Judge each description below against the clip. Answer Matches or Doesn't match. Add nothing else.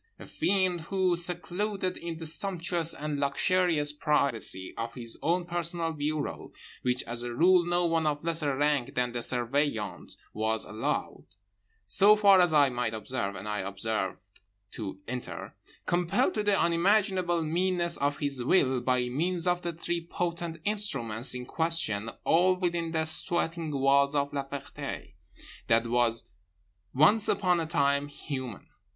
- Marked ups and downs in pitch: Matches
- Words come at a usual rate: Matches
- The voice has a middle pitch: Matches